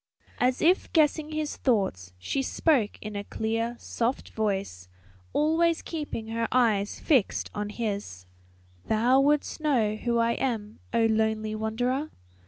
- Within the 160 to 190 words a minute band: No, slow, 135 wpm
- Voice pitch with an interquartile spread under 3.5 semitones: No, average, 4.3 semitones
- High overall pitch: Yes, high, 230 Hz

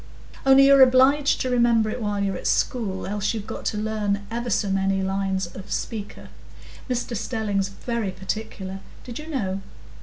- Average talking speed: Yes, average, 160 wpm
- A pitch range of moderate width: Yes, average, 3.7 semitones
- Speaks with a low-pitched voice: No, high, 210 Hz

